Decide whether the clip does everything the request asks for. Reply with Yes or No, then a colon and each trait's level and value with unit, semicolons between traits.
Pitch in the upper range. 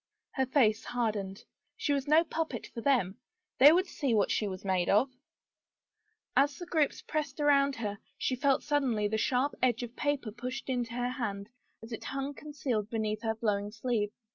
Yes: high, 245 Hz